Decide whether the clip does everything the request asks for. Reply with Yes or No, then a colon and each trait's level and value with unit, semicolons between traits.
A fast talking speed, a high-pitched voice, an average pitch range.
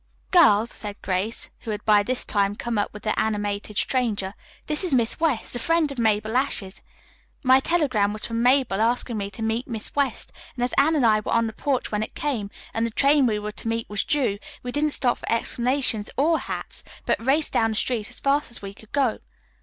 Yes: fast, 225 wpm; high, 230 Hz; average, 4.2 semitones